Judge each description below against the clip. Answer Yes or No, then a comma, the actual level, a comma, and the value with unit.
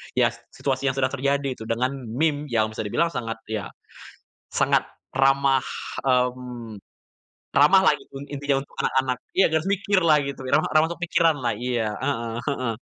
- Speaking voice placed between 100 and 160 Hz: Yes, low, 135 Hz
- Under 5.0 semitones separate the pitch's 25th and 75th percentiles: Yes, average, 2.8 semitones